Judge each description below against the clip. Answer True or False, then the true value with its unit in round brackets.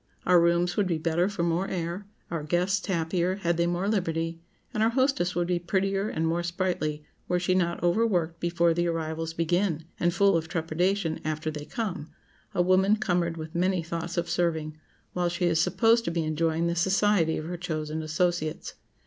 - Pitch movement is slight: True (2.2 semitones)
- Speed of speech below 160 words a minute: False (185 wpm)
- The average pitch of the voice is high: False (170 Hz)